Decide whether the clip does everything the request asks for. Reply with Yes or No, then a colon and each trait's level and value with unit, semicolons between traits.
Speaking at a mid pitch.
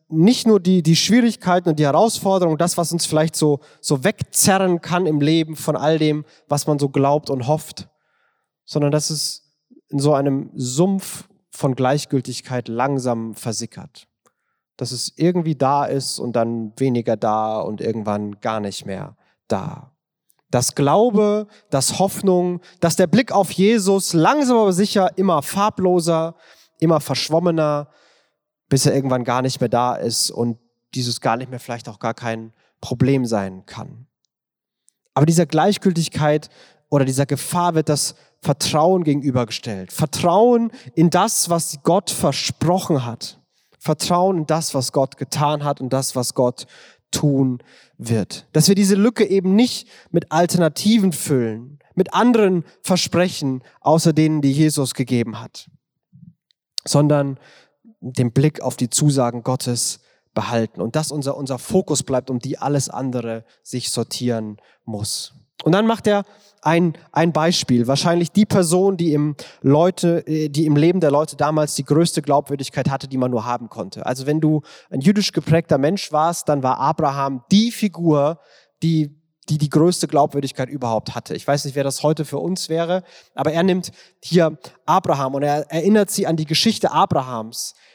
Yes: medium, 150 Hz